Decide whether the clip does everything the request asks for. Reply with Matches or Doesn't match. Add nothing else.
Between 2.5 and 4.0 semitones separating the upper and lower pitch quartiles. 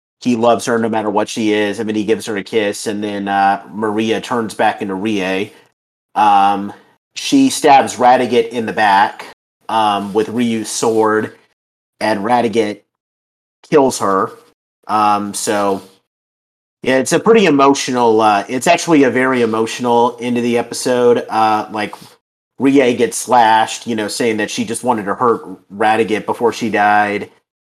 Matches